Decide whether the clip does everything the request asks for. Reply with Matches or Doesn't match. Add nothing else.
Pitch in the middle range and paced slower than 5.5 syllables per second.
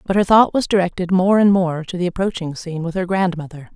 Doesn't match